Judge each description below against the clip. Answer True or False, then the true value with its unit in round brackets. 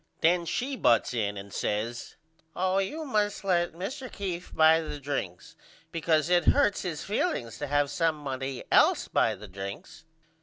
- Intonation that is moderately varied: False (6.6 semitones)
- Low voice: False (160 Hz)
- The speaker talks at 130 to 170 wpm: True (155 wpm)